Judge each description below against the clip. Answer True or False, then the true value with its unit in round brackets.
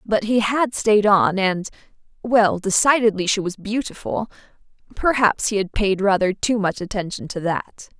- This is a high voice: True (205 Hz)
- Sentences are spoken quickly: False (145 wpm)